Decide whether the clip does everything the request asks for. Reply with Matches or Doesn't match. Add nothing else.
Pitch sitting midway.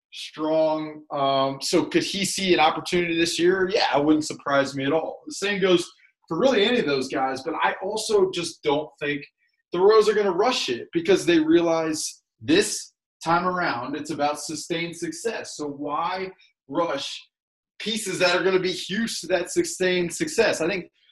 Matches